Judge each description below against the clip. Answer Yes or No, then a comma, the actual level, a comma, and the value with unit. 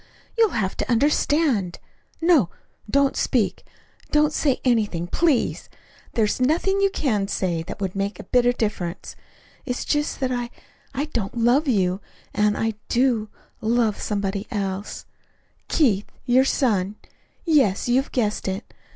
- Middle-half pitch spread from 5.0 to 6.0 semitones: Yes, wide, 5.4 semitones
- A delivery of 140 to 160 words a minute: Yes, average, 145 wpm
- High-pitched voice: Yes, high, 235 Hz